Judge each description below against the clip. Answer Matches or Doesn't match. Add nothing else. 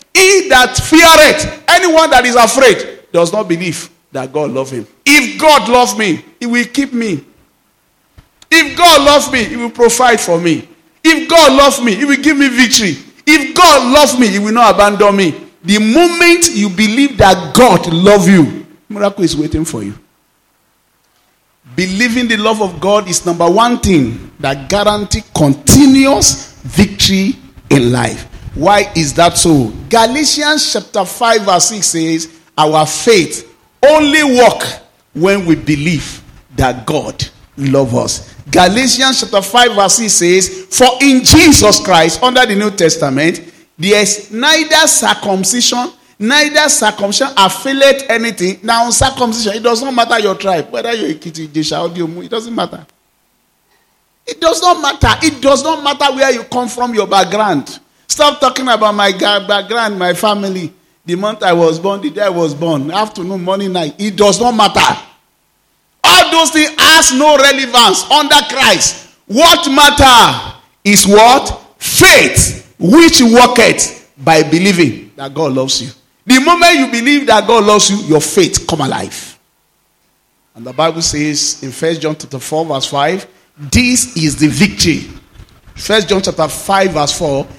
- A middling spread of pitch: Doesn't match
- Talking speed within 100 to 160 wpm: Matches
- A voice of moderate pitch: Doesn't match